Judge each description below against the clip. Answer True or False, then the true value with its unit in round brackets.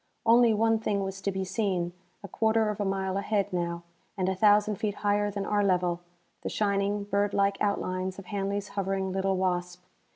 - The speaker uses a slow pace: False (190 wpm)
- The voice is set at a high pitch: True (200 Hz)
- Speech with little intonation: True (1.6 semitones)